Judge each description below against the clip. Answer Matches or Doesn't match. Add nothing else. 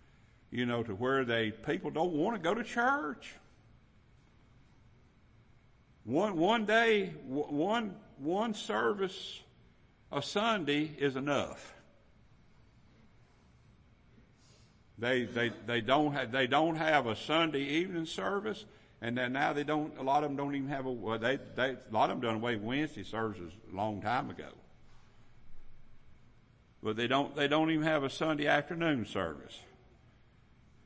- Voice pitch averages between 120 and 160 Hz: Matches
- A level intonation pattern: Doesn't match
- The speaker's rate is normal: Matches